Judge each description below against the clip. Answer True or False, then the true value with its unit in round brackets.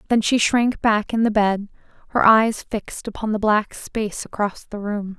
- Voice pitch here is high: True (215 Hz)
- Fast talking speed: False (195 wpm)